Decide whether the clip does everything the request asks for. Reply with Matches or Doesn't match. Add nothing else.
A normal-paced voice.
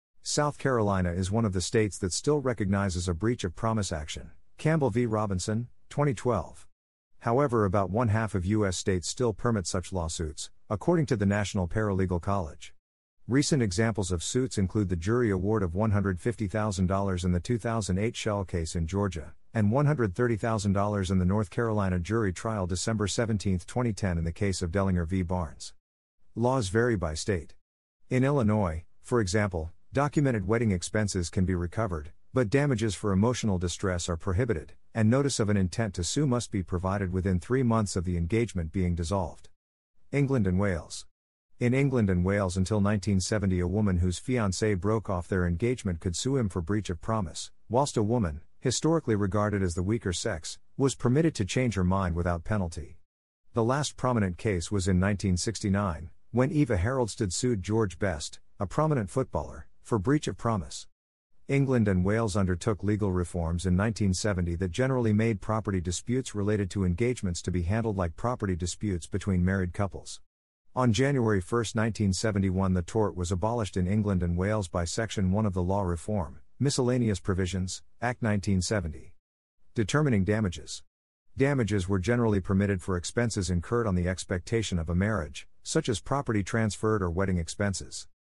Matches